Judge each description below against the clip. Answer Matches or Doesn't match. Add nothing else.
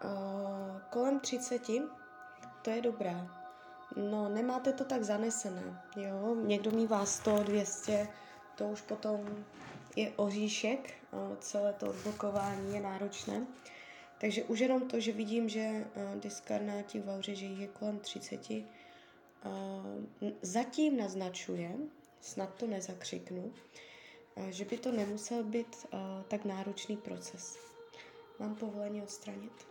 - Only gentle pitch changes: Doesn't match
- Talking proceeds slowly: Matches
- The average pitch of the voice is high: Matches